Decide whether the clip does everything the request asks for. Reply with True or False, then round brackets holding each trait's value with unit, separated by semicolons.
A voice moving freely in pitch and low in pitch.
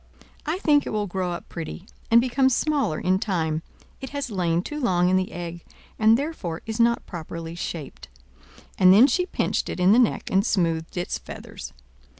False (6.0 semitones; 190 Hz)